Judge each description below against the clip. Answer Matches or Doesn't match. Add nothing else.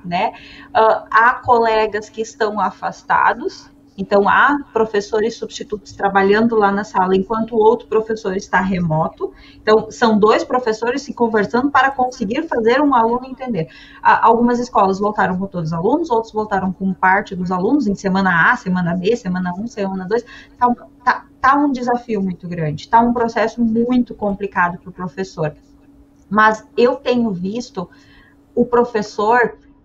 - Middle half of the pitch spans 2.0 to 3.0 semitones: Doesn't match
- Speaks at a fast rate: Doesn't match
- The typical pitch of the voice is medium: Doesn't match